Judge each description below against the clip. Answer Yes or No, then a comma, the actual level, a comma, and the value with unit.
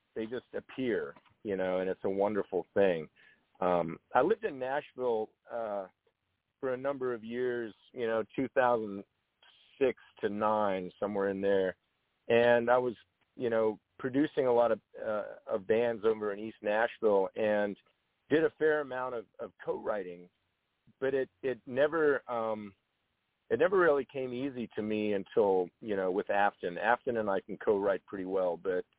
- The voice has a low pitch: Yes, low, 120 Hz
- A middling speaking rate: Yes, average, 160 wpm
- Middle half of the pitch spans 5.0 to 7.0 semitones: Yes, wide, 5.5 semitones